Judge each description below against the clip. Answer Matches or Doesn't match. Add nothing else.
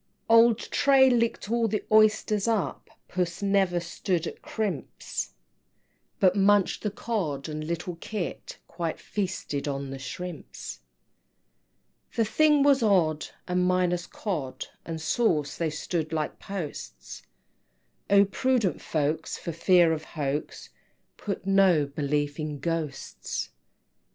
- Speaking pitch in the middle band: Matches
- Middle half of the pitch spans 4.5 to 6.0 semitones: Matches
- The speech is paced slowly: Matches